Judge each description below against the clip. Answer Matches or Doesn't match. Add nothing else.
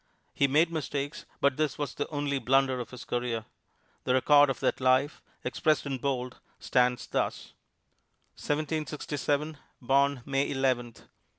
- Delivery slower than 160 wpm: Matches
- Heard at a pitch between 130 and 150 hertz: Matches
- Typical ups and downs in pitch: Doesn't match